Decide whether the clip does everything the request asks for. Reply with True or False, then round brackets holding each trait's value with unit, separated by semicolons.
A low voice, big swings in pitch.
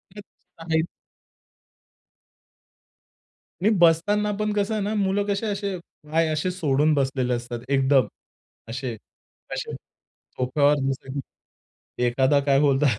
False (150 Hz; 6.7 semitones)